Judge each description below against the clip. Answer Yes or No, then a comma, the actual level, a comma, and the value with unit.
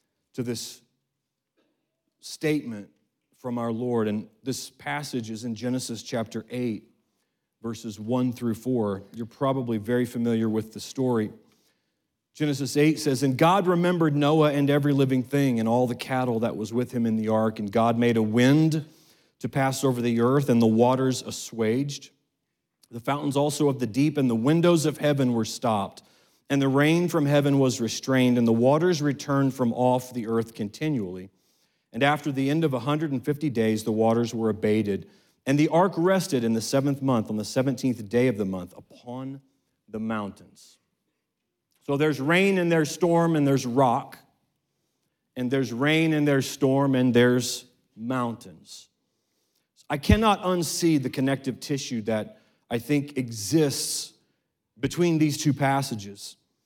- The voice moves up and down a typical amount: Yes, average, 3.9 semitones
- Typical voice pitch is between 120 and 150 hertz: Yes, low, 130 Hz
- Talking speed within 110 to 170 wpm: Yes, average, 160 wpm